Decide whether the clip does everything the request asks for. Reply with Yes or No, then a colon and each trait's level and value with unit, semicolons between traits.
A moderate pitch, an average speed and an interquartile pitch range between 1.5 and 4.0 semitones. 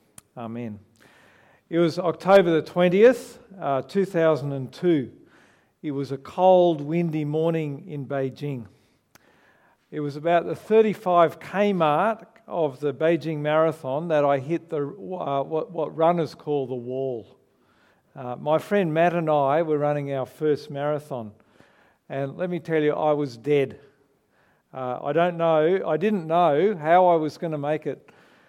Yes: medium, 155 Hz; average, 145 wpm; average, 3.6 semitones